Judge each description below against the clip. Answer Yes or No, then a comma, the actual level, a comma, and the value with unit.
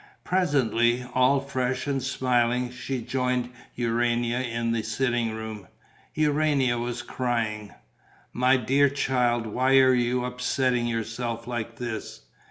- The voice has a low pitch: Yes, low, 125 Hz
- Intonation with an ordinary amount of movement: No, narrow, 1.8 semitones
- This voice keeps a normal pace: No, slow, 120 wpm